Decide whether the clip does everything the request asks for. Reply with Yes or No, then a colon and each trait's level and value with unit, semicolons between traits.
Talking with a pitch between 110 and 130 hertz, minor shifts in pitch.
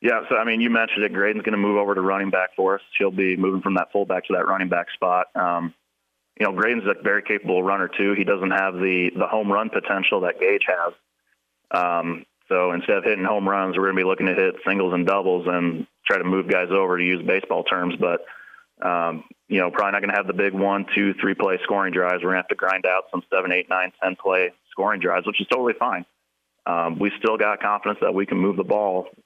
No: very low, 95 Hz; narrow, 1.9 semitones